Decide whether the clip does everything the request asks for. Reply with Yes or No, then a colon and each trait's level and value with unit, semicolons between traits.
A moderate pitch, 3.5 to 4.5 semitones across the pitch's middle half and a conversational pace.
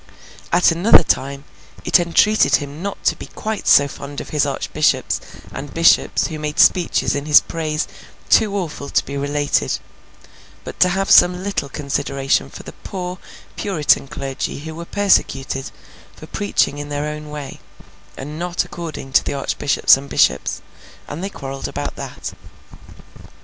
Yes: medium, 150 Hz; average, 3.9 semitones; average, 155 wpm